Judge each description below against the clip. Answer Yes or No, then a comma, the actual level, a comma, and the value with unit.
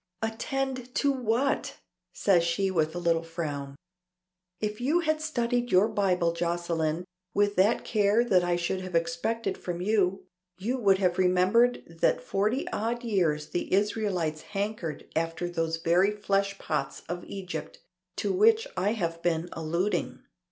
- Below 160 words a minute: Yes, average, 145 wpm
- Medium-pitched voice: No, high, 195 Hz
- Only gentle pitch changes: No, average, 4.8 semitones